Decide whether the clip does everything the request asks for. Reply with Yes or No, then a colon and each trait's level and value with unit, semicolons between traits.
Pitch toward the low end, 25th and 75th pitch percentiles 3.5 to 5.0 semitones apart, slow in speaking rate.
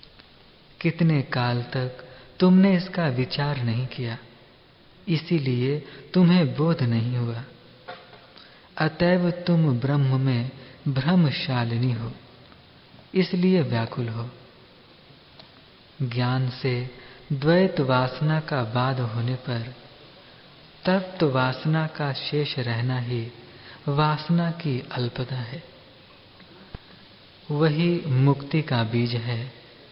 Yes: low, 130 Hz; average, 4.3 semitones; slow, 90 wpm